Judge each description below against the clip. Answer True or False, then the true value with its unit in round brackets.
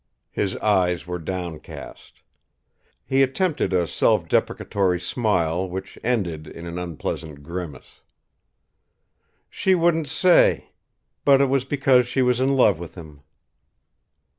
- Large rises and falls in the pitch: True (7.5 semitones)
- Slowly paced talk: True (120 wpm)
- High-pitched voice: False (95 Hz)